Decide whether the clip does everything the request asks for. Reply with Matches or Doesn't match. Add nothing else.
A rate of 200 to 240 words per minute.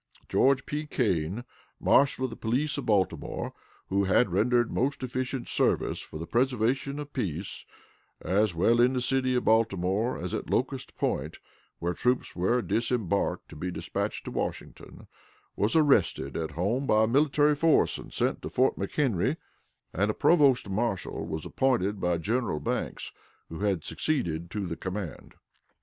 Doesn't match